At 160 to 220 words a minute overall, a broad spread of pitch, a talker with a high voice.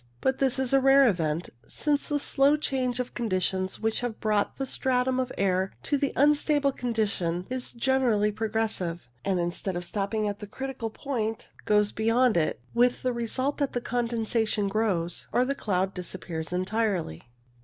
No: average, 170 wpm; average, 5.0 semitones; high, 225 Hz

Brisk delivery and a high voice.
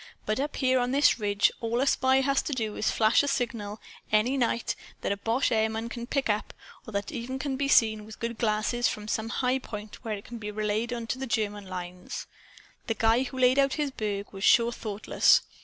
Yes: fast, 225 wpm; high, 230 Hz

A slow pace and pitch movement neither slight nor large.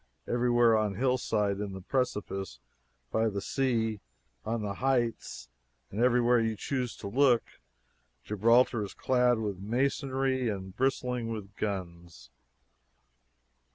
Yes: slow, 115 wpm; average, 3.8 semitones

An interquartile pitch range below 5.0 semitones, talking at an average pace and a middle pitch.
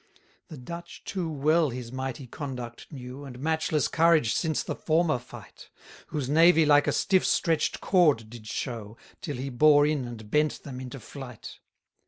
Yes: average, 4.2 semitones; average, 170 wpm; medium, 145 Hz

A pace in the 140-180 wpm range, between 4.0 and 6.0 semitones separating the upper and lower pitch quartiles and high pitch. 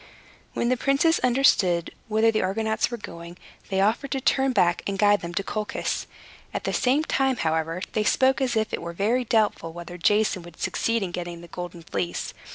No: average, 195 wpm; wide, 5.5 semitones; high, 205 Hz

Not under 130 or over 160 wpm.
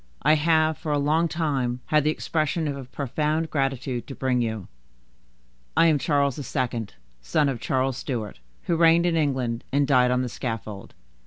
No: average, 175 wpm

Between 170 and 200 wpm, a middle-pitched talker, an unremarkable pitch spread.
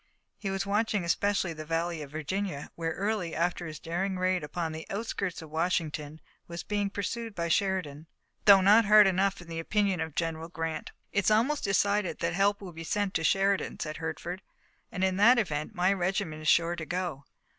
Yes: average, 190 wpm; medium, 180 Hz; average, 3.5 semitones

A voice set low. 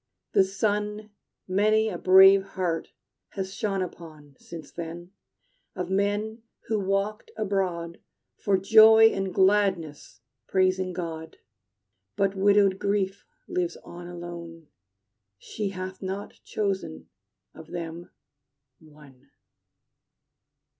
No: high, 190 Hz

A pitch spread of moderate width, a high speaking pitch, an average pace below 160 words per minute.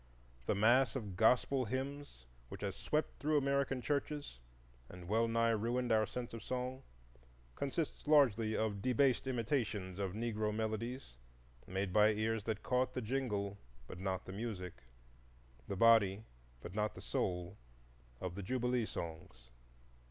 No: average, 4.2 semitones; low, 110 Hz; average, 145 wpm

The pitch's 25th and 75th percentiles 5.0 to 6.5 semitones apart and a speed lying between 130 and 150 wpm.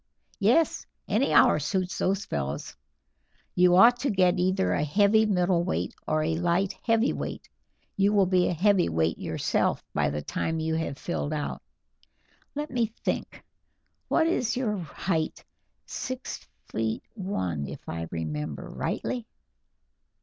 Yes: wide, 5.6 semitones; slow, 135 wpm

